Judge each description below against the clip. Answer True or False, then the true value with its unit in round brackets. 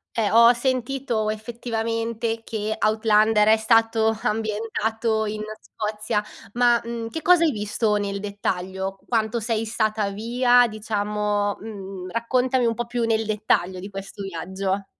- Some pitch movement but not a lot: False (1.9 semitones)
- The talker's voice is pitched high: True (220 Hz)